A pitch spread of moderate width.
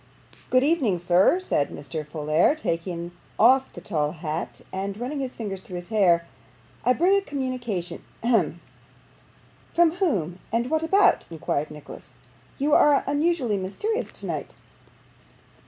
No: wide, 9.0 semitones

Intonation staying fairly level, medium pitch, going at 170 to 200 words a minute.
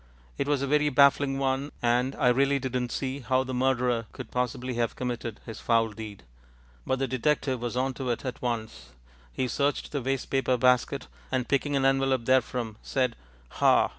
No: narrow, 2.0 semitones; low, 130 Hz; average, 180 wpm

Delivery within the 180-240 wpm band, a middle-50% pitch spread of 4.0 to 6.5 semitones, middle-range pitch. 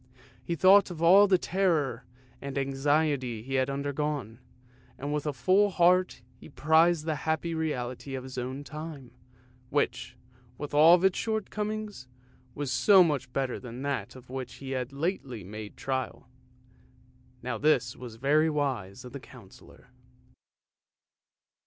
No: average, 140 wpm; average, 4.3 semitones; medium, 145 Hz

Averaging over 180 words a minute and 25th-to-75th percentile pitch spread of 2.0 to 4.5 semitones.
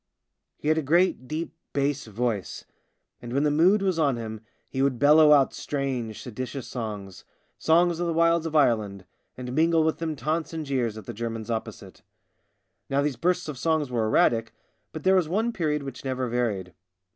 No: average, 190 wpm; average, 5.3 semitones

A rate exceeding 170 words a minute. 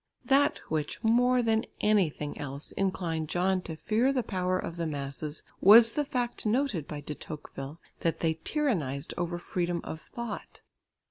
No: average, 155 wpm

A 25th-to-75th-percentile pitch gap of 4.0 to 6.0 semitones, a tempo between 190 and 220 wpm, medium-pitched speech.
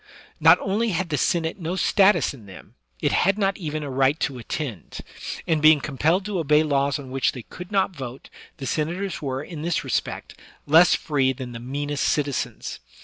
Yes: average, 4.5 semitones; average, 195 wpm; medium, 150 Hz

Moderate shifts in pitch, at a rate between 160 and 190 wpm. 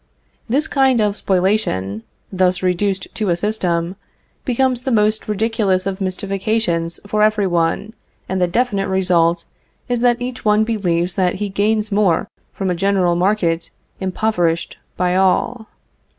No: average, 3.3 semitones; average, 145 wpm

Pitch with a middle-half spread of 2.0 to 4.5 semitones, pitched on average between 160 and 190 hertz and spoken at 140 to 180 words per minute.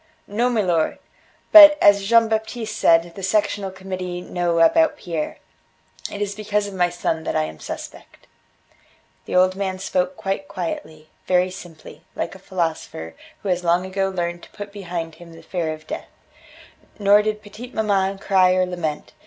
Yes: average, 2.9 semitones; medium, 185 Hz; average, 170 wpm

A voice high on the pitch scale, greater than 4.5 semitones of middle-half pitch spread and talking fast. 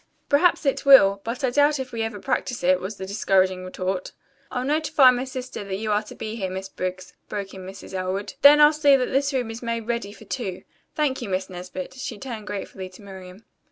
Yes: high, 215 Hz; wide, 5.5 semitones; fast, 225 wpm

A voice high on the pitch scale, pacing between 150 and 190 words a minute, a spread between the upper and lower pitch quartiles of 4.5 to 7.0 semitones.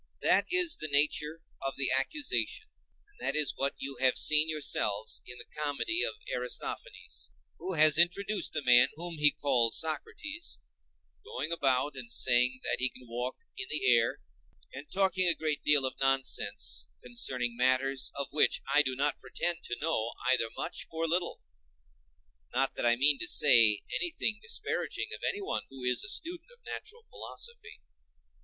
No: medium, 140 Hz; average, 160 wpm; wide, 5.4 semitones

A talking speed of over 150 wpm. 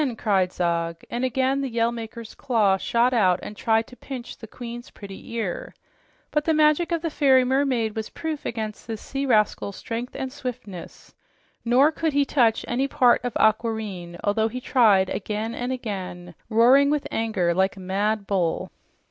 Yes: average, 175 wpm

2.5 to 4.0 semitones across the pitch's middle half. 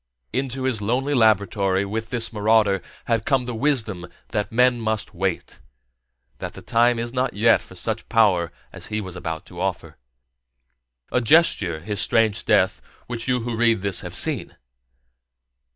Yes: average, 3.3 semitones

